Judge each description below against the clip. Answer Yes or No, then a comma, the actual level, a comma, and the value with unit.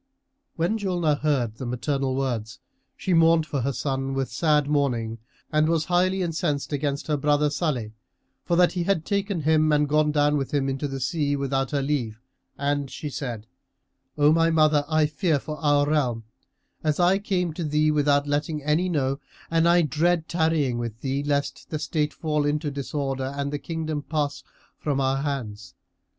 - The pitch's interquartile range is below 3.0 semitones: Yes, narrow, 2.6 semitones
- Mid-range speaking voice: Yes, medium, 150 Hz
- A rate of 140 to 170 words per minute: No, average, 180 wpm